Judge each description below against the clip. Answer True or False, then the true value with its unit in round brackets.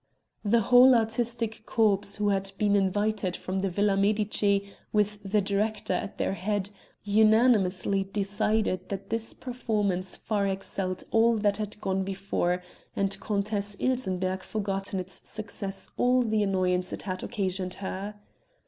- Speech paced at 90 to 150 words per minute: True (140 wpm)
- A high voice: True (200 Hz)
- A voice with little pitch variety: True (2.0 semitones)